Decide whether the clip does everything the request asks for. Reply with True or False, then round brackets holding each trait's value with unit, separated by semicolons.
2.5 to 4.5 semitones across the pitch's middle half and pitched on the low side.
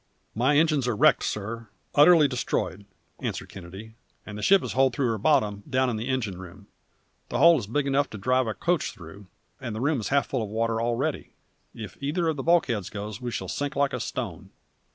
False (5.1 semitones; 120 Hz)